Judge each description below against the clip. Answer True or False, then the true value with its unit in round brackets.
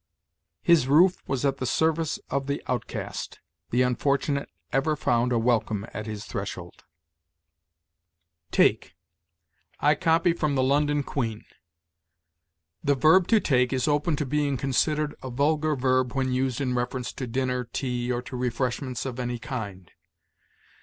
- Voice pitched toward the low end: True (130 Hz)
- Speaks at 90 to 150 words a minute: True (145 wpm)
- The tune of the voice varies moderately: True (3.1 semitones)